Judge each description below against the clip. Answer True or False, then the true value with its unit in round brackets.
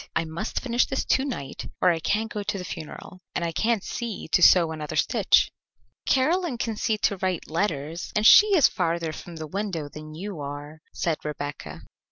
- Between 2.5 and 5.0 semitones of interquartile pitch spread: False (5.6 semitones)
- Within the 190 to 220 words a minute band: True (195 wpm)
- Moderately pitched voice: True (180 Hz)